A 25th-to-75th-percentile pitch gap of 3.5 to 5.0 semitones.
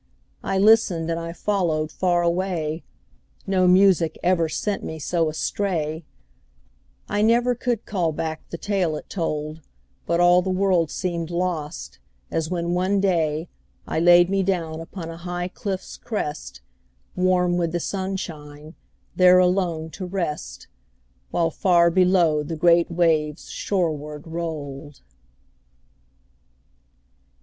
No: narrow, 2.6 semitones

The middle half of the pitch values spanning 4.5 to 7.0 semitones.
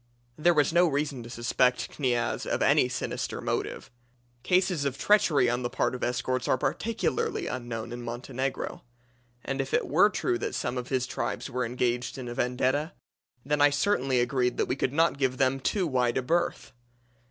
No: average, 3.3 semitones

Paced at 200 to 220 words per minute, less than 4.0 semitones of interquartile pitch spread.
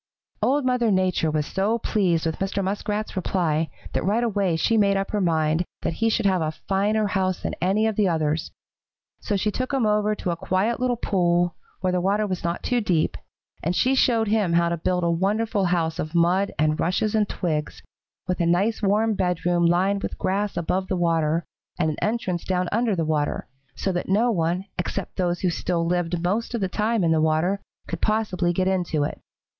Yes: fast, 205 wpm; average, 3.6 semitones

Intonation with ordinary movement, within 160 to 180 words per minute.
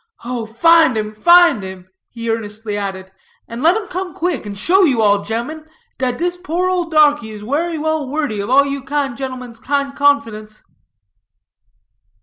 No: wide, 6.4 semitones; average, 165 wpm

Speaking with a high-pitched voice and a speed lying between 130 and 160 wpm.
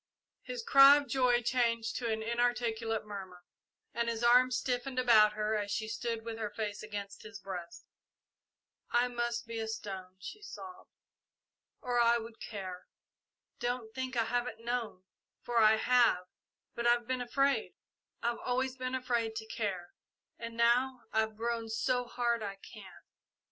Yes: high, 235 Hz; average, 155 wpm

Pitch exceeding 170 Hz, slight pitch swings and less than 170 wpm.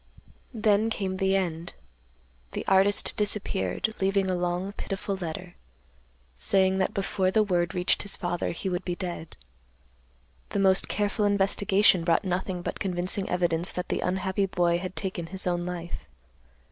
Yes: high, 190 Hz; narrow, 1.9 semitones; average, 150 wpm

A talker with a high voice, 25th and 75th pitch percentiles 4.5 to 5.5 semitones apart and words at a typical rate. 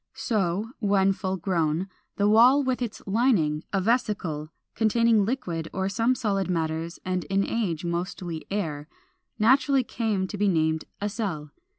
Yes: high, 195 Hz; average, 4.9 semitones; average, 150 wpm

